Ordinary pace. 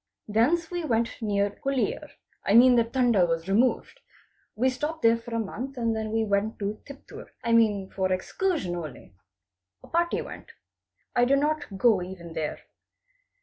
Yes: average, 150 wpm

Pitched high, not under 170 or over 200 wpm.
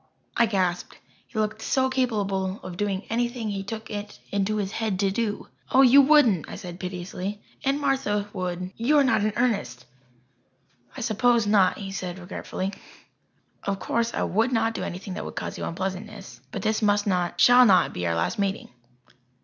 Yes: high, 205 Hz; average, 180 wpm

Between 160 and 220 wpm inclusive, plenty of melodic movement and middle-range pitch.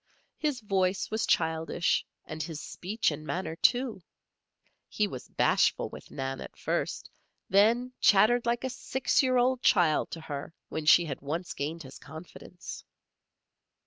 No: average, 145 wpm; wide, 6.9 semitones; medium, 180 Hz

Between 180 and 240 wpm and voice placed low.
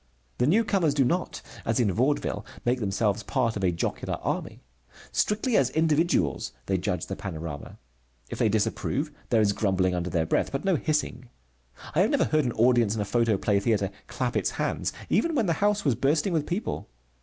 Yes: average, 190 wpm; low, 120 Hz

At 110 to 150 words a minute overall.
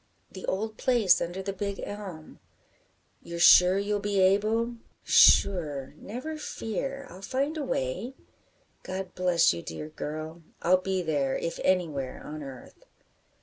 Yes: average, 140 wpm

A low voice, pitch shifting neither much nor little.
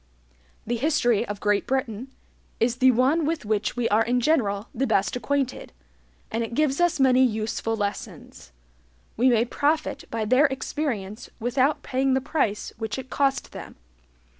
No: very high, 250 Hz; average, 3.6 semitones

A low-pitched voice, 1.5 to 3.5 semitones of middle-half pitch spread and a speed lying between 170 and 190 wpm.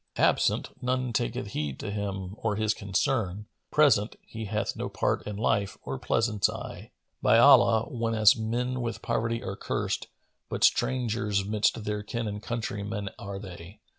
No: low, 105 Hz; narrow, 2.4 semitones; average, 155 wpm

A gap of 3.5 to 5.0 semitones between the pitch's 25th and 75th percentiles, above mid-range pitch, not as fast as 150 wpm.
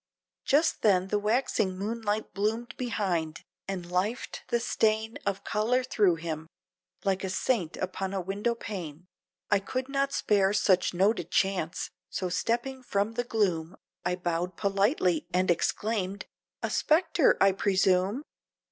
Yes: average, 3.8 semitones; high, 200 Hz; average, 140 wpm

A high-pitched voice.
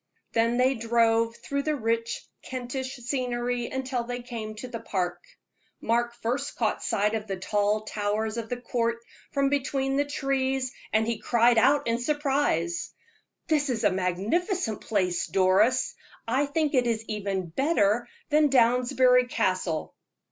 Yes: high, 235 Hz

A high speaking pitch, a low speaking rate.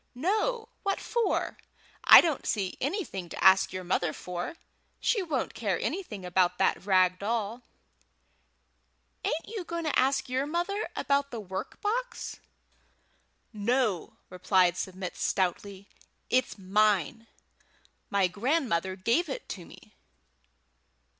Yes: high, 215 Hz; slow, 120 wpm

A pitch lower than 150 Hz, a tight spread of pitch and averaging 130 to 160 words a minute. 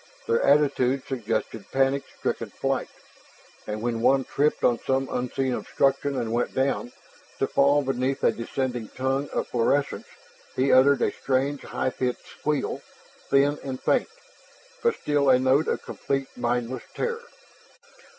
Yes: low, 135 Hz; narrow, 2.0 semitones; average, 140 wpm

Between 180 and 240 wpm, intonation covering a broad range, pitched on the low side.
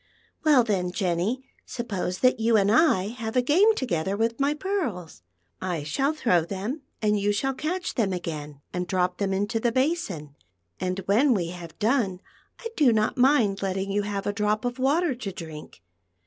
No: average, 195 wpm; wide, 5.8 semitones; high, 210 Hz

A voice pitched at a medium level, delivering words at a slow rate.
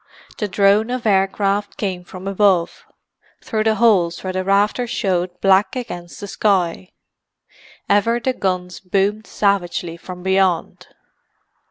No: high, 195 Hz; slow, 130 wpm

